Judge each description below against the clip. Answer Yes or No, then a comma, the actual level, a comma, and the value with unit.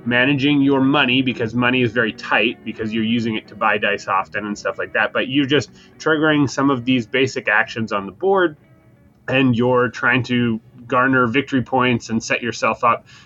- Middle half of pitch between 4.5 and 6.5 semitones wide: No, average, 3.0 semitones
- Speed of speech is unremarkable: Yes, average, 195 wpm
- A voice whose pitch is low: Yes, low, 125 Hz